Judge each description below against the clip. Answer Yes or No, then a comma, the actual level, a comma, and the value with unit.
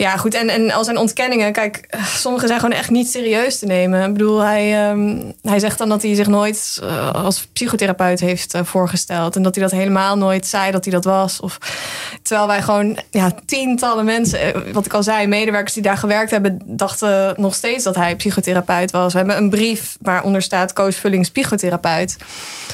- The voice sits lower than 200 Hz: No, high, 205 Hz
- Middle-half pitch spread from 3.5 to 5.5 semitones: No, narrow, 2.4 semitones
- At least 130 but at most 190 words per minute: No, fast, 200 wpm